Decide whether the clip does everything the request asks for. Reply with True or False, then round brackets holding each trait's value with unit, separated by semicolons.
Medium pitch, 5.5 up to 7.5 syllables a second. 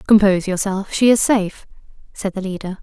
False (200 Hz; 5.9 syllables/s)